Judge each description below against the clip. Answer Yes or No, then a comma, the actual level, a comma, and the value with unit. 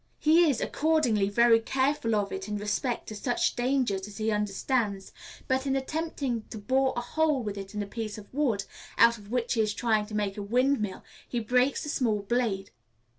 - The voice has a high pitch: Yes, high, 230 Hz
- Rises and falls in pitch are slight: No, average, 4.0 semitones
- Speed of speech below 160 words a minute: No, average, 200 wpm